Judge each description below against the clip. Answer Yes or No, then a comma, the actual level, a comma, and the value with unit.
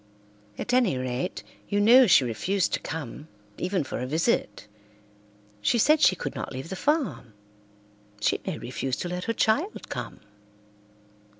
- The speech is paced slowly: No, average, 155 wpm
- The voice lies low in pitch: No, medium, 180 Hz